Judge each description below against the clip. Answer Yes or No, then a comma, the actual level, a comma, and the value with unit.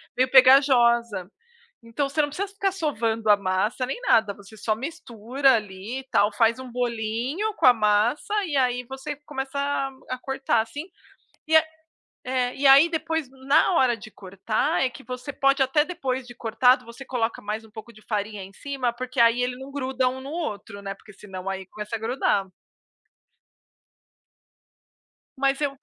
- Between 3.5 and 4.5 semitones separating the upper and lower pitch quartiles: Yes, average, 3.8 semitones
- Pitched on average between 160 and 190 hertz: No, very high, 250 Hz